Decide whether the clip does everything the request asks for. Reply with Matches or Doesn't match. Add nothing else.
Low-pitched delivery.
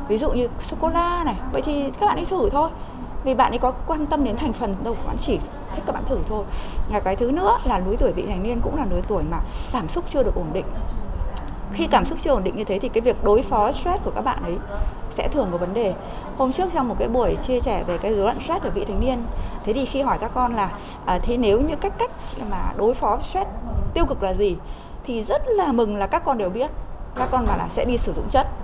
Doesn't match